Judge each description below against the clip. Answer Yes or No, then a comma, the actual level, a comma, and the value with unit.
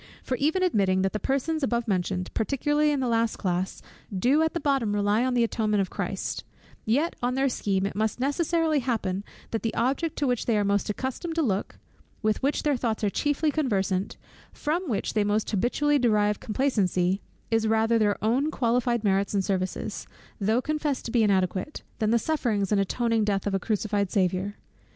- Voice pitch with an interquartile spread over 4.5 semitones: Yes, average, 5.2 semitones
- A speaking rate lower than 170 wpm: No, average, 190 wpm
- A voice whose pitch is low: No, high, 225 Hz